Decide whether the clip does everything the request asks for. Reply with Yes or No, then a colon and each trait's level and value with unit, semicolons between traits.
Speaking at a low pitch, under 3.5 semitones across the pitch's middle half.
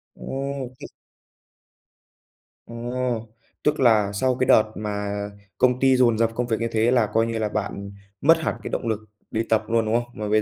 Yes: low, 115 Hz; average, 2.8 semitones